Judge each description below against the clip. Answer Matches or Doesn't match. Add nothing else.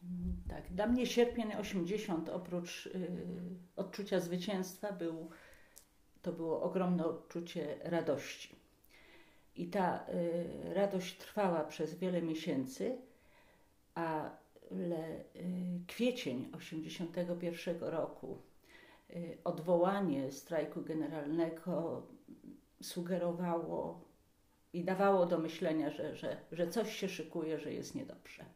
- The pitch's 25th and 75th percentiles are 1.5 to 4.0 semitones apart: Matches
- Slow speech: Matches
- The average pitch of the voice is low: Doesn't match